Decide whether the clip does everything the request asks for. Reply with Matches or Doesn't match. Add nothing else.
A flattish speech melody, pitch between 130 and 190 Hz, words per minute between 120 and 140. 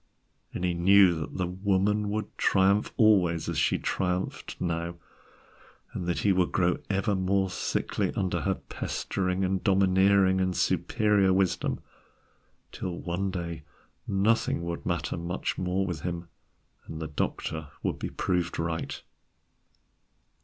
Doesn't match